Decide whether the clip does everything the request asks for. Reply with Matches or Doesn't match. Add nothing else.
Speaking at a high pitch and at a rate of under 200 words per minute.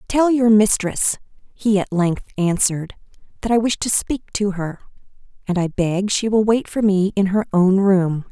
Matches